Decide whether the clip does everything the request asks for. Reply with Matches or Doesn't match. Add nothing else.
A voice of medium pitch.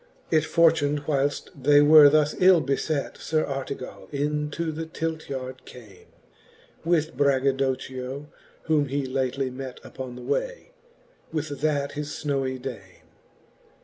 Matches